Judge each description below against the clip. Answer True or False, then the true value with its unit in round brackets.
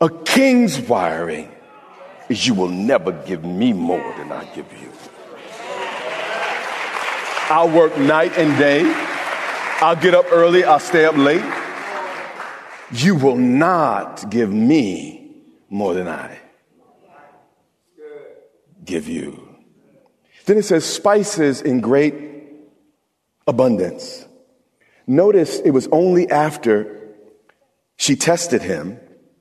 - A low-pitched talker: False (170 Hz)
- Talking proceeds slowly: True (105 wpm)